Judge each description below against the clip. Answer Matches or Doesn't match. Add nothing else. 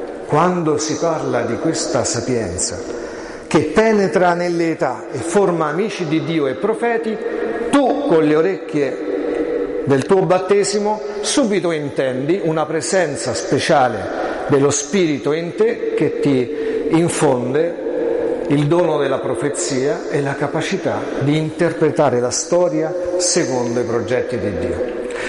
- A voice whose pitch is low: Doesn't match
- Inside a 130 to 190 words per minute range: Doesn't match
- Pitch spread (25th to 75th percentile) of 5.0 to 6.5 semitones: Matches